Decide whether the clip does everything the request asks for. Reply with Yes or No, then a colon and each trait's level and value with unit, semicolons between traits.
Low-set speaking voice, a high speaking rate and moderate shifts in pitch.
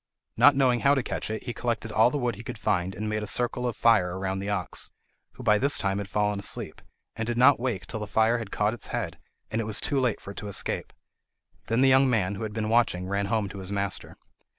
Yes: low, 110 Hz; fast, 260 wpm; average, 3.1 semitones